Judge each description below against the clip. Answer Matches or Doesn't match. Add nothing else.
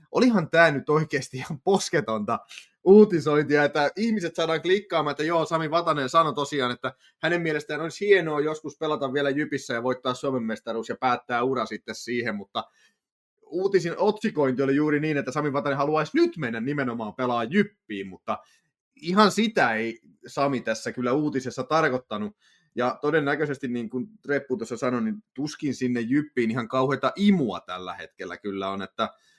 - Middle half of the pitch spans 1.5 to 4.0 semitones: Doesn't match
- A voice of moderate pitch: Matches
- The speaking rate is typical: Doesn't match